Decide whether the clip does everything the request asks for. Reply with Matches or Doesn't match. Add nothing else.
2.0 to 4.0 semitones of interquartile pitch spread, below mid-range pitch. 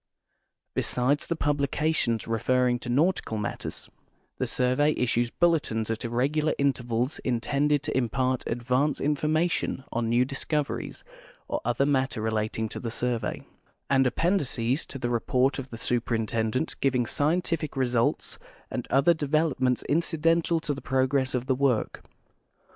Matches